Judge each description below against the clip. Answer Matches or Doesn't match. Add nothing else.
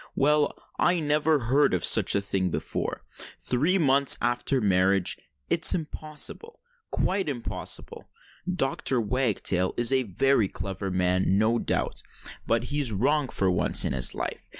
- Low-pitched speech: Matches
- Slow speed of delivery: Matches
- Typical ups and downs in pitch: Doesn't match